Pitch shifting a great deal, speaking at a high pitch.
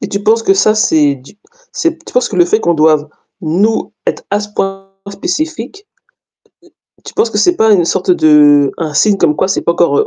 Yes: wide, 5.8 semitones; high, 195 Hz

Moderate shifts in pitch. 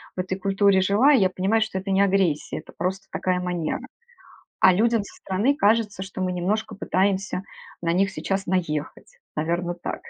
No: narrow, 1.9 semitones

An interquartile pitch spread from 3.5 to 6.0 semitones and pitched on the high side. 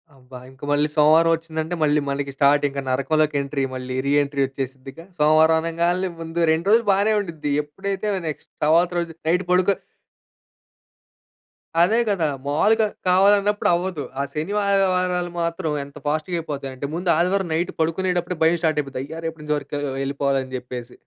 No: average, 4.2 semitones; medium, 160 Hz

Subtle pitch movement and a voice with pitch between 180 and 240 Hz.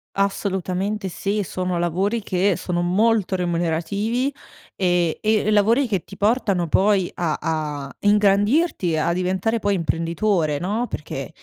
No: average, 3.4 semitones; high, 190 Hz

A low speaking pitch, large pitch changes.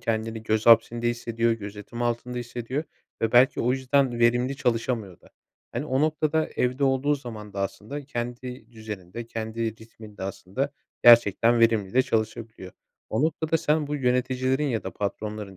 No: low, 120 Hz; average, 2.8 semitones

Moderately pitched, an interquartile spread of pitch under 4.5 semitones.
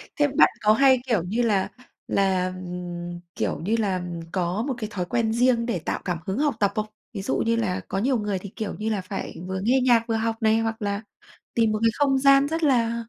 No: high, 220 Hz; average, 3.6 semitones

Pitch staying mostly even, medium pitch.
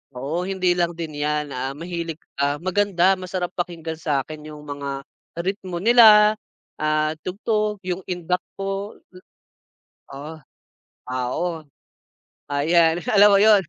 No: average, 4.0 semitones; medium, 175 Hz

